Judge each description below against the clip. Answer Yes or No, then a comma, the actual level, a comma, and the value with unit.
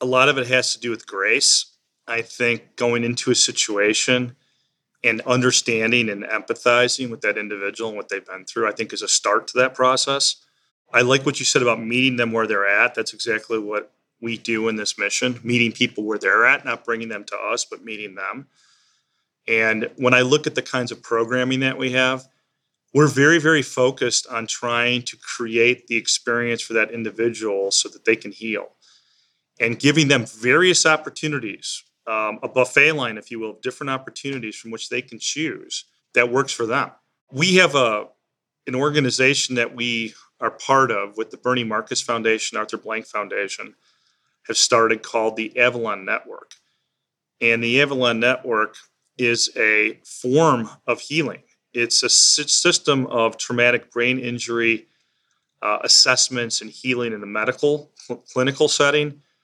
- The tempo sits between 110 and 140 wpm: No, average, 170 wpm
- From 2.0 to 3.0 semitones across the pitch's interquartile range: Yes, narrow, 2.4 semitones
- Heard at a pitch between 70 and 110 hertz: No, low, 120 Hz